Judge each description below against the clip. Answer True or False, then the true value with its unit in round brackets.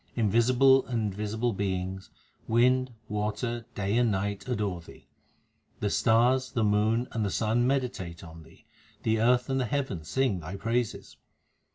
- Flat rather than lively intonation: False (3.5 semitones)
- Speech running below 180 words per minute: True (150 wpm)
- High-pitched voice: False (110 Hz)